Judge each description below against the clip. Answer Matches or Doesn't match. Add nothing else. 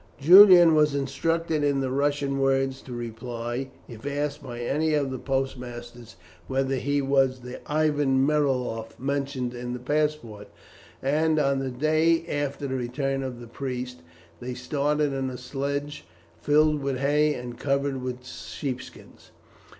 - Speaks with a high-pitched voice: Doesn't match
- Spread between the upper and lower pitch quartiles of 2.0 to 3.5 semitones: Matches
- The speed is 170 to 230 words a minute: Doesn't match